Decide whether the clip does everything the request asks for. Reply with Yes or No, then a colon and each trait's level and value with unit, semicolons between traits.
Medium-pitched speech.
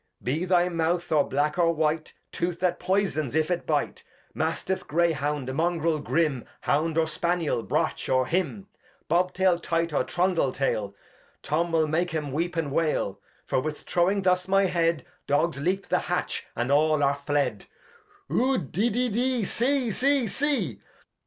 Yes: medium, 165 Hz